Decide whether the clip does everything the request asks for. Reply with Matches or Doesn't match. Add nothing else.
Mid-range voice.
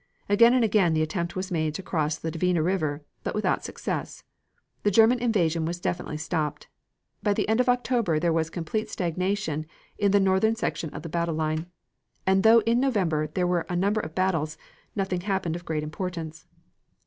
Matches